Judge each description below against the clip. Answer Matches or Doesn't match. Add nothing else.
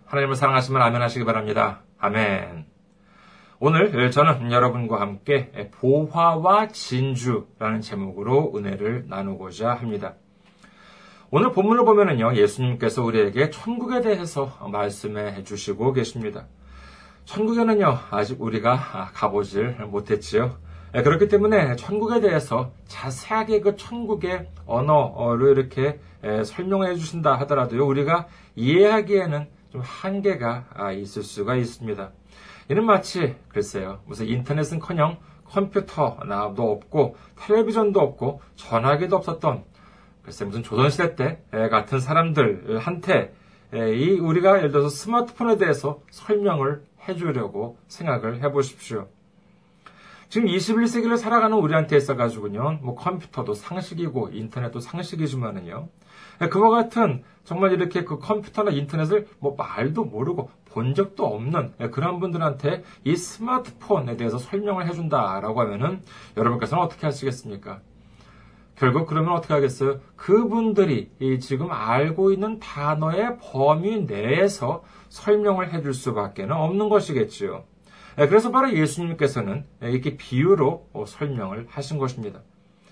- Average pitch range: Doesn't match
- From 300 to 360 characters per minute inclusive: Matches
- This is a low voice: Doesn't match